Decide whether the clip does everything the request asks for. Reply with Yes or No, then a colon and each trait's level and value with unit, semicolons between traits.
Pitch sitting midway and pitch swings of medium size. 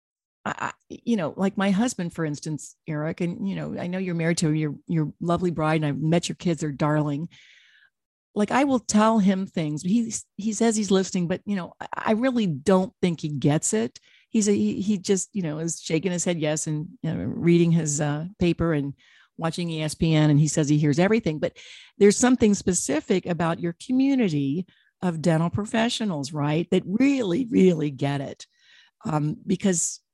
Yes: medium, 175 Hz; average, 4.8 semitones